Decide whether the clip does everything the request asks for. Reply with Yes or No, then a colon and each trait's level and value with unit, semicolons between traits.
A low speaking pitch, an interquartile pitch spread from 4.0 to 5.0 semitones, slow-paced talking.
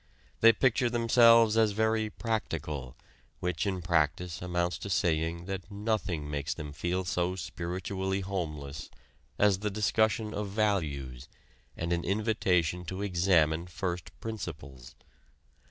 Yes: very low, 90 Hz; average, 4.3 semitones; slow, 120 wpm